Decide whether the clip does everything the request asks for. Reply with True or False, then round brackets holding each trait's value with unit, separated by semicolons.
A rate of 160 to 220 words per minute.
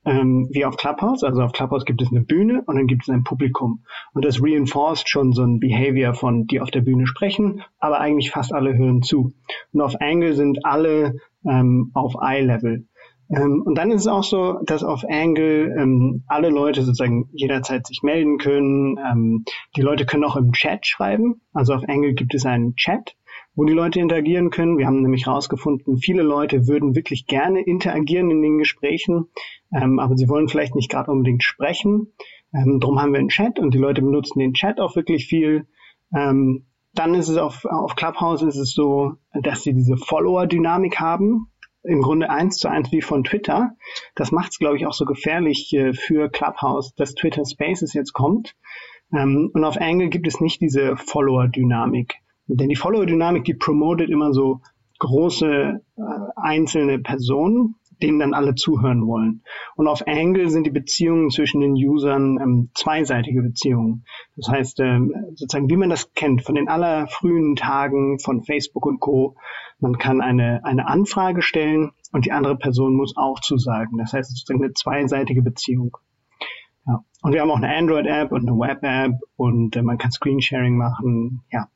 True (185 wpm)